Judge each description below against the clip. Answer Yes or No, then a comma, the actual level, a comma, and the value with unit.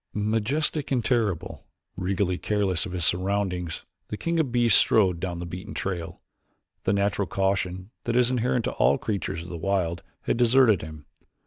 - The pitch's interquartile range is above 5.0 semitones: No, average, 4.4 semitones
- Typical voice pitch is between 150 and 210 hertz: No, low, 100 Hz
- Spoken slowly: No, average, 170 wpm